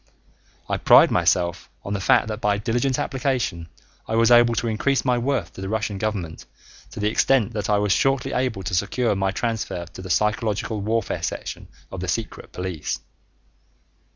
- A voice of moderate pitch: No, low, 110 Hz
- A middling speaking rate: Yes, average, 180 wpm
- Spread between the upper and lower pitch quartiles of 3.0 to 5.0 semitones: Yes, average, 3.7 semitones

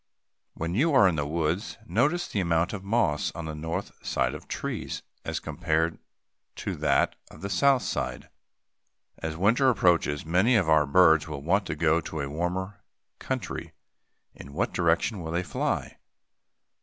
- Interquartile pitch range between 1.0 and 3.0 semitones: No, average, 3.9 semitones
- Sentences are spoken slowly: No, average, 165 wpm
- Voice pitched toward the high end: No, very low, 85 Hz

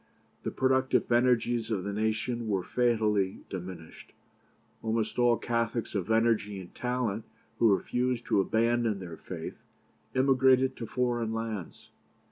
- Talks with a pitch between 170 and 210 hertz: No, low, 115 Hz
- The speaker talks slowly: Yes, slow, 125 wpm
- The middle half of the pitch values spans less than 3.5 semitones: Yes, average, 2.8 semitones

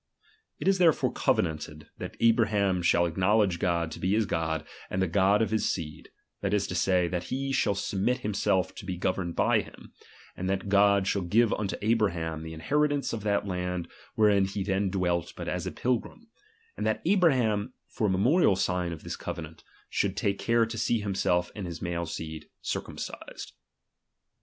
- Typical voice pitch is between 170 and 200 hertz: No, very low, 95 Hz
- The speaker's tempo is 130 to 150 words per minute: No, average, 185 wpm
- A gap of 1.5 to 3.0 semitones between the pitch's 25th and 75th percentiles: No, average, 3.7 semitones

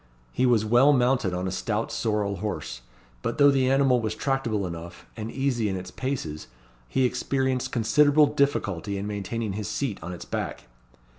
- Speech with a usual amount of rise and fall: Yes, average, 4.9 semitones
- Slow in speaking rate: No, average, 170 wpm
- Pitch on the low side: Yes, low, 115 Hz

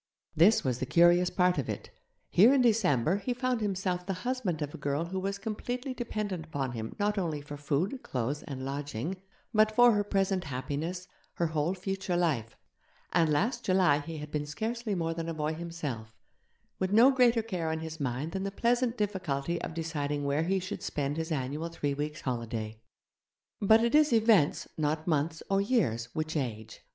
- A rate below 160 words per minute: No, average, 185 wpm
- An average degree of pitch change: No, wide, 5.7 semitones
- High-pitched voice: No, medium, 170 Hz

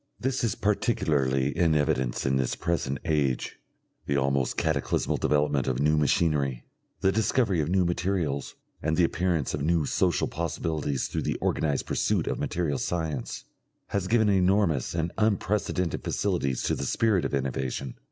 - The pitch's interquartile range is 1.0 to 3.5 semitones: No, average, 4.8 semitones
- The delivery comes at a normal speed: Yes, average, 150 wpm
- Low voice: Yes, very low, 80 Hz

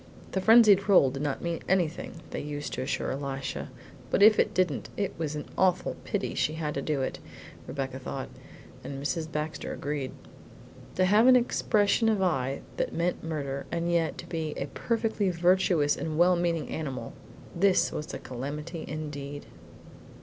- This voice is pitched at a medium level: Yes, medium, 160 Hz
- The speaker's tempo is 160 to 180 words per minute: Yes, average, 170 wpm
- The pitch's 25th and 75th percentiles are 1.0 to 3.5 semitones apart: No, average, 4.5 semitones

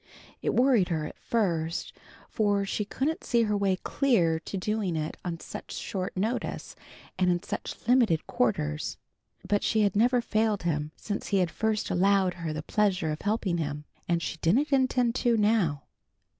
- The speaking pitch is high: Yes, high, 200 Hz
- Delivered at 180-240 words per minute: No, average, 170 wpm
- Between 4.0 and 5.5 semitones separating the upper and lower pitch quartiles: Yes, average, 4.9 semitones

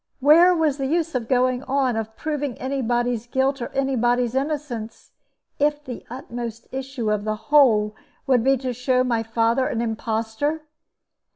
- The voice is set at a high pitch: Yes, very high, 255 Hz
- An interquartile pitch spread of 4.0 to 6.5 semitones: No, average, 3.1 semitones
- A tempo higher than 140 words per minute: Yes, average, 165 wpm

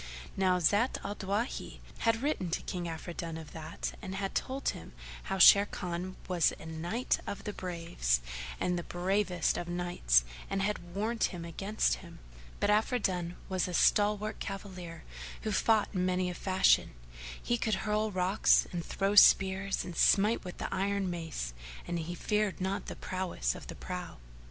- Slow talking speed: No, average, 165 wpm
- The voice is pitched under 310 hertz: Yes, medium, 185 Hz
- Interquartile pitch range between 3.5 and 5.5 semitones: No, average, 2.8 semitones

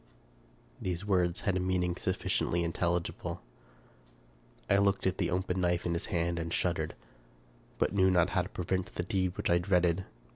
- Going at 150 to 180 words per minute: Yes, average, 170 wpm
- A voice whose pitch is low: Yes, very low, 90 Hz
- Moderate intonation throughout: No, narrow, 1.4 semitones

